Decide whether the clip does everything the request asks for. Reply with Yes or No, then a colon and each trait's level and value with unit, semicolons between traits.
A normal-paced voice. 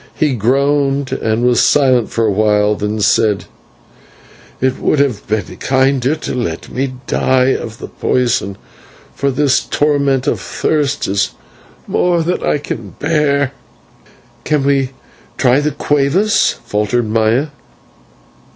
No: slow, 130 wpm